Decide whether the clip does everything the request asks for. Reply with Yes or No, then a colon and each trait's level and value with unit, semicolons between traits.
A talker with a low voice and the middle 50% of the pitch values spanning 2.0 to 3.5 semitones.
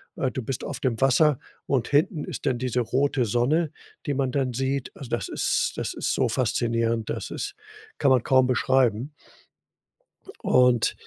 Yes: low, 130 Hz; narrow, 2.5 semitones